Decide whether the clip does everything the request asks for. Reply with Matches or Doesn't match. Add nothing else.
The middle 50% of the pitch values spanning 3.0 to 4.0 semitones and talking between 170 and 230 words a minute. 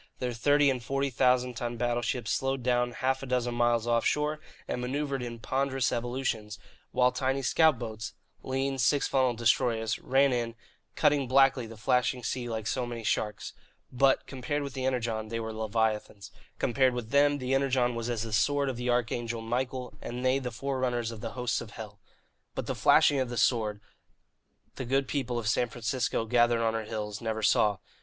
Doesn't match